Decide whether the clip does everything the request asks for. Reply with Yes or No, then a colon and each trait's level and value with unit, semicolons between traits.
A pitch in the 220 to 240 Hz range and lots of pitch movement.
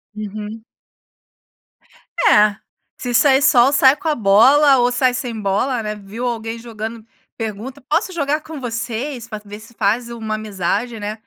No: high, 230 Hz; average, 3.5 semitones